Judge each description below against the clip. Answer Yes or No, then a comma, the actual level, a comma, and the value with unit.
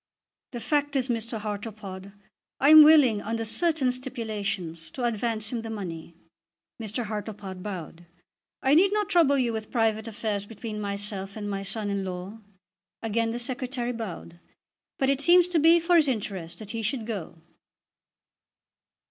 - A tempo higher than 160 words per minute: No, average, 155 wpm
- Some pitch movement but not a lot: Yes, average, 4.3 semitones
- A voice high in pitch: Yes, high, 225 Hz